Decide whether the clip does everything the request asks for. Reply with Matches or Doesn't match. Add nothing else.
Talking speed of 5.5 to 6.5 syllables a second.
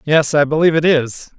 Matches